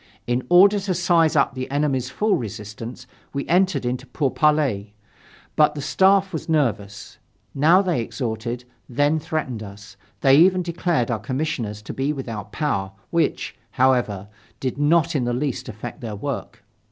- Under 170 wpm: Yes, average, 155 wpm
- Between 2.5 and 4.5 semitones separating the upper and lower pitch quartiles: No, average, 5.3 semitones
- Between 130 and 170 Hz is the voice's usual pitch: Yes, low, 135 Hz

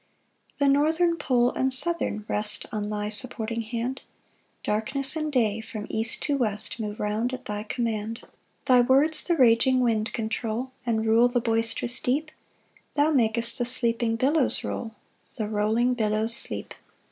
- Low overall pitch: No, high, 235 Hz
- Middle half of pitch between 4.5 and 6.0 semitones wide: No, average, 3.1 semitones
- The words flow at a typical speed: Yes, average, 160 wpm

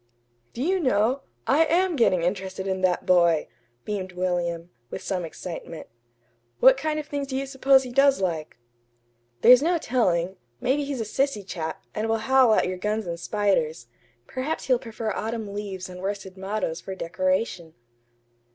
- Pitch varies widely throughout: Yes, wide, 6.4 semitones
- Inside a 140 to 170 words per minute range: Yes, average, 165 wpm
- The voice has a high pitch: Yes, high, 205 Hz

